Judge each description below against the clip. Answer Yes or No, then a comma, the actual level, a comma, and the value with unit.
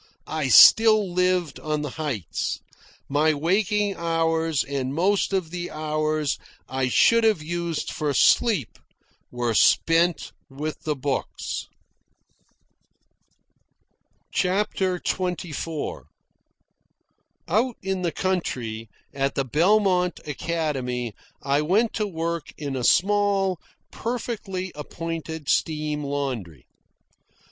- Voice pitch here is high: No, medium, 165 Hz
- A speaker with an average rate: No, slow, 100 wpm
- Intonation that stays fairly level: No, average, 4.5 semitones